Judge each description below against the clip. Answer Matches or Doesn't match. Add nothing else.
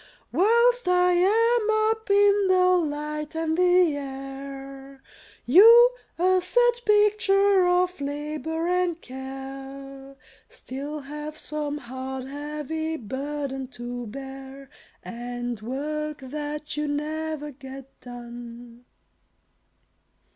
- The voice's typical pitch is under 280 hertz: Doesn't match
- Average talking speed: Doesn't match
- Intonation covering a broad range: Doesn't match